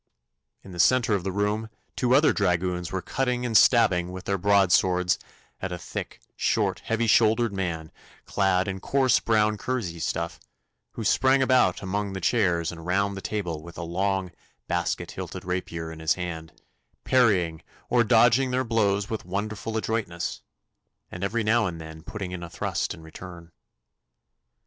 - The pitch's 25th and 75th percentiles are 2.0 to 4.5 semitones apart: Yes, average, 4.1 semitones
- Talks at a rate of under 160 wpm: No, average, 165 wpm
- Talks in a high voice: No, very low, 95 Hz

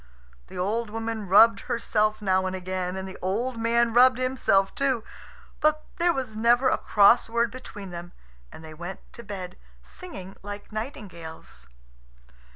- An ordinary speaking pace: Yes, average, 155 wpm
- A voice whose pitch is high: Yes, high, 215 Hz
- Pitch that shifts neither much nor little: Yes, average, 4.0 semitones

